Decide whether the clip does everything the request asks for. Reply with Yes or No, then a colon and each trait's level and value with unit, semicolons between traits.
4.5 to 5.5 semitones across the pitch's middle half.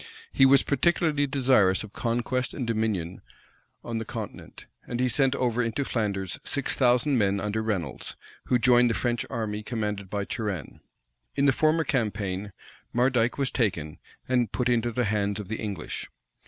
No: average, 3.6 semitones